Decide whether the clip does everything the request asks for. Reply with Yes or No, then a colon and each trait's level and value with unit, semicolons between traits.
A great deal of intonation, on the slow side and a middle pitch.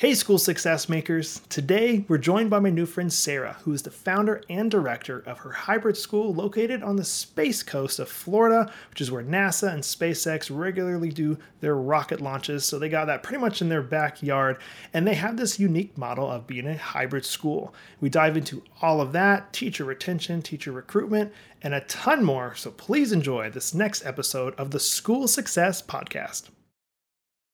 No: wide, 5.8 semitones; average, 185 wpm; medium, 165 Hz